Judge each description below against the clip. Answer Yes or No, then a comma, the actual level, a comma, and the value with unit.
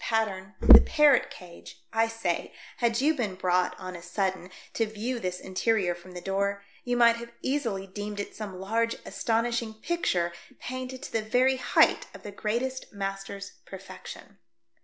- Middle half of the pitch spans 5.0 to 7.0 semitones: No, average, 3.7 semitones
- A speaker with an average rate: Yes, average, 165 wpm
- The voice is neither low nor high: No, high, 210 Hz